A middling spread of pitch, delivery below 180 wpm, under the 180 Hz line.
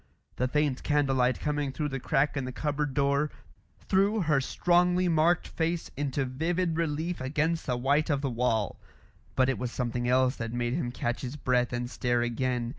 No: average, 3.7 semitones; average, 190 wpm; low, 135 Hz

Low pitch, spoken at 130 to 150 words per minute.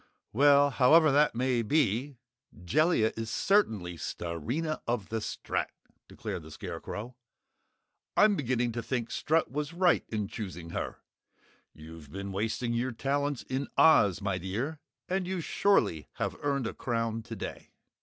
Yes: low, 120 Hz; average, 140 wpm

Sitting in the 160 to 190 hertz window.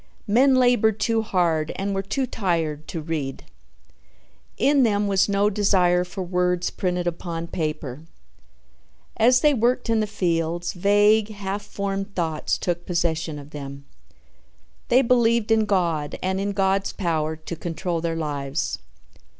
Yes: medium, 185 Hz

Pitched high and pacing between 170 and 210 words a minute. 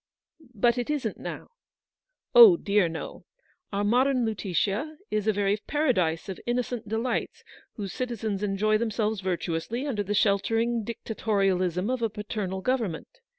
No: high, 215 Hz; average, 140 wpm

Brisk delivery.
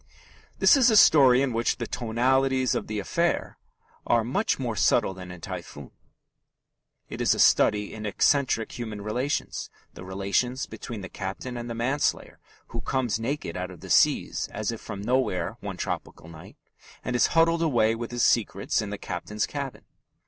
No: average, 175 wpm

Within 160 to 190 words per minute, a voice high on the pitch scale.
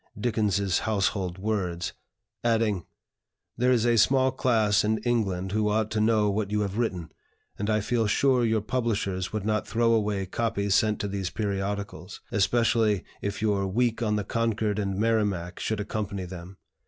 No: average, 165 wpm; low, 105 Hz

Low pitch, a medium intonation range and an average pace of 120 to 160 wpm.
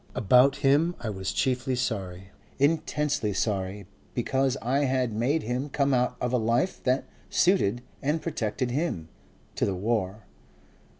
Yes: low, 125 Hz; average, 4.5 semitones; average, 140 wpm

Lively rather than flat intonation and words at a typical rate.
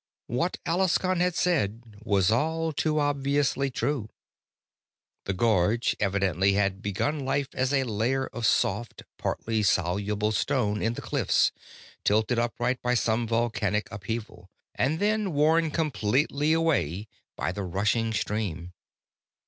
No: wide, 5.8 semitones; slow, 125 wpm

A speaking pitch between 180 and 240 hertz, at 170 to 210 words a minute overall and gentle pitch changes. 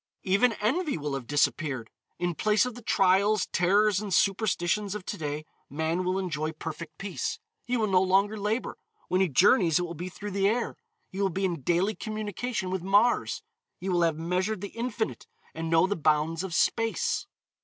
No: high, 190 Hz; average, 185 wpm; average, 4.1 semitones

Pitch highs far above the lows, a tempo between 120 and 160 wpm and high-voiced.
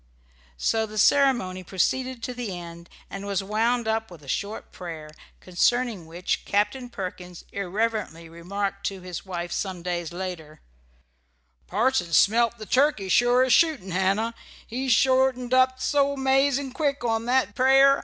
Yes: wide, 5.9 semitones; average, 145 wpm; high, 215 Hz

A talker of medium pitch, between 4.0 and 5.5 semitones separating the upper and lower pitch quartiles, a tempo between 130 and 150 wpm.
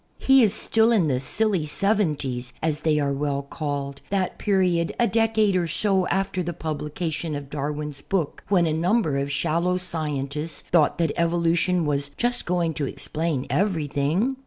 No: medium, 165 Hz; average, 4.3 semitones; average, 160 wpm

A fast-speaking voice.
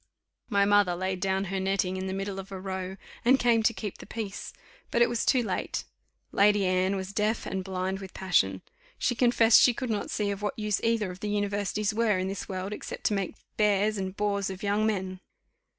Yes: fast, 215 wpm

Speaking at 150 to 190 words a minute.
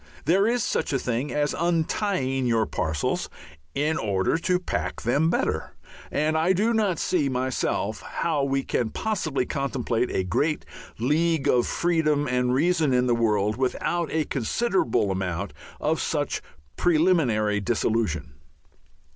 No: average, 140 wpm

